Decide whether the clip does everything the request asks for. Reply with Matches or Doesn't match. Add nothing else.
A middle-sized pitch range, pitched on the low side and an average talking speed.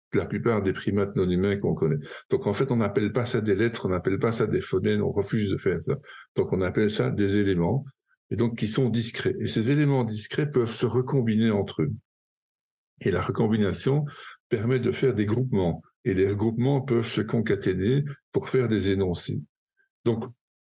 Matches